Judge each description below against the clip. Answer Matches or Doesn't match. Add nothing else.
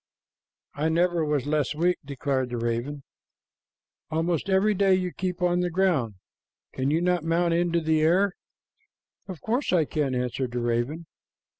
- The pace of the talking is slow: Doesn't match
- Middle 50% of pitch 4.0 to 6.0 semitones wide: Matches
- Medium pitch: Matches